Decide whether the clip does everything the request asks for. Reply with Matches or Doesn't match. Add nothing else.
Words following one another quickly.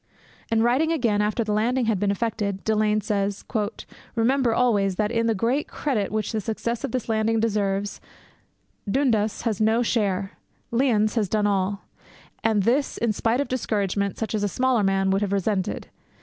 Doesn't match